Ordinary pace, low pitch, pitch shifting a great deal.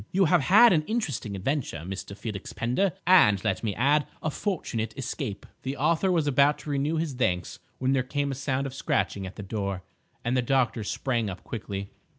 Yes: average, 195 wpm; low, 130 Hz; wide, 6.1 semitones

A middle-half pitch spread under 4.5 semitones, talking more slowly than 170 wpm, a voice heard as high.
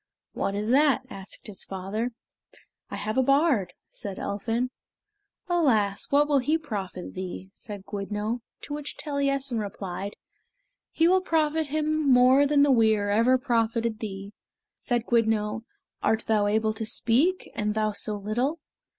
No: average, 5.3 semitones; average, 145 wpm; high, 230 Hz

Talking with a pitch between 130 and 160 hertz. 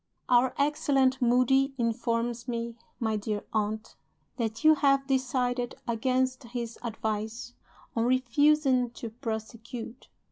No: high, 245 Hz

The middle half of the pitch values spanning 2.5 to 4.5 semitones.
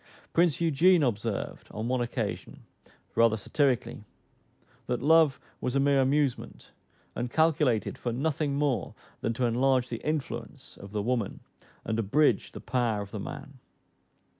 Yes: average, 4.0 semitones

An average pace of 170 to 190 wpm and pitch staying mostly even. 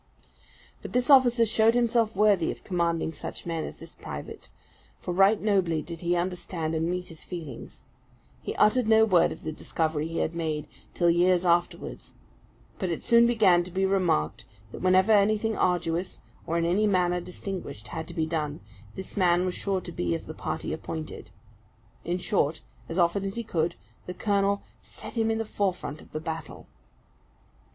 No: average, 180 wpm; average, 3.5 semitones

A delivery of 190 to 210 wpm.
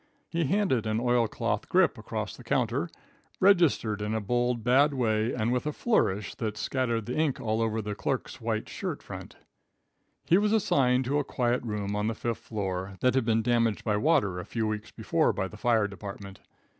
Yes: average, 195 wpm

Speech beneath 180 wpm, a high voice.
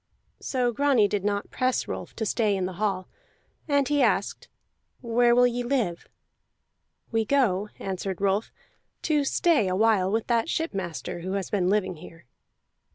Yes: average, 160 wpm; high, 215 Hz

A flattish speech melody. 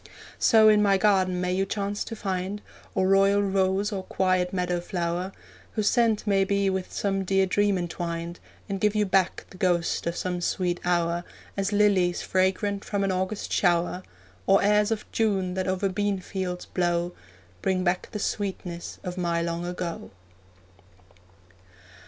Yes: narrow, 2.0 semitones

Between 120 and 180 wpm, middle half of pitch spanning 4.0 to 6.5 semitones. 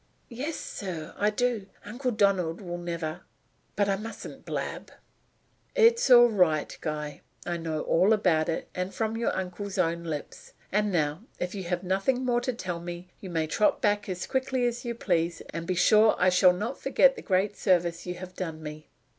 No: average, 190 wpm; average, 4.4 semitones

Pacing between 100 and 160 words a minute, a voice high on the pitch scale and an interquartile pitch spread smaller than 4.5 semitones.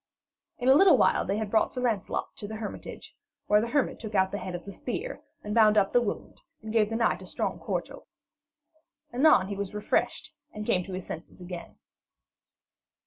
No: fast, 205 wpm; high, 210 Hz; average, 3.2 semitones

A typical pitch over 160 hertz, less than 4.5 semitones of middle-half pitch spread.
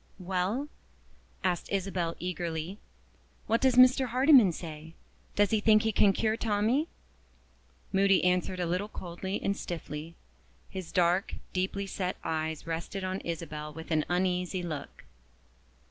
Yes: medium, 185 Hz; average, 3.4 semitones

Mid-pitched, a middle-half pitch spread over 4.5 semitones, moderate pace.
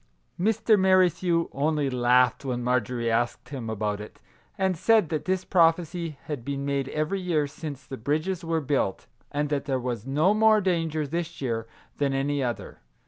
Yes: medium, 145 Hz; average, 5.2 semitones; average, 175 wpm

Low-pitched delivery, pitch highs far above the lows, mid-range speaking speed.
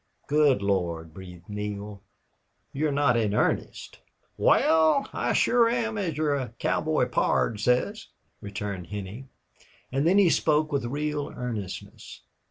No: low, 125 Hz; wide, 7.0 semitones; slow, 125 wpm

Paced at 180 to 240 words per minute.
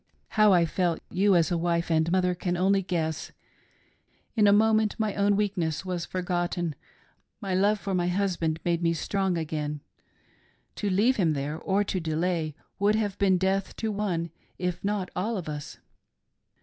No: average, 170 wpm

